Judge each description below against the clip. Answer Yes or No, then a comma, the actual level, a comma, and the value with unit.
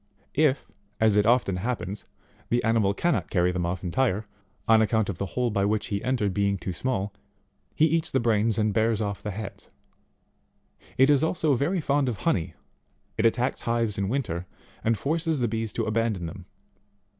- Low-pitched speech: Yes, low, 110 Hz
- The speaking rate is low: No, average, 185 wpm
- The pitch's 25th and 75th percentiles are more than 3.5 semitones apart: Yes, average, 4.0 semitones